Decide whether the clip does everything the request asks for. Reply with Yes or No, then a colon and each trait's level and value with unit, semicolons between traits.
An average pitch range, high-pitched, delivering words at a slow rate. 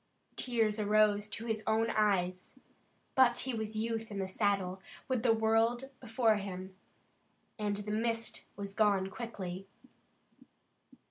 No: narrow, 2.2 semitones; high, 215 Hz; slow, 130 wpm